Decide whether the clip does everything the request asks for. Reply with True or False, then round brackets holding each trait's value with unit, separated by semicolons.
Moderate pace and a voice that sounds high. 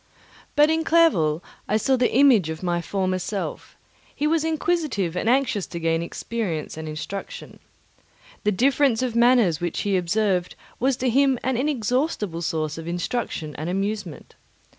True (155 wpm; 210 Hz)